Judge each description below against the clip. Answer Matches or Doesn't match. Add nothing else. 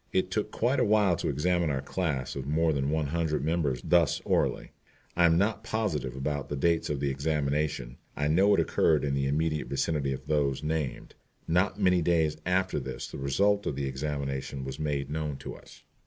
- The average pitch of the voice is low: Matches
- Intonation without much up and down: Doesn't match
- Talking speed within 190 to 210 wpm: Matches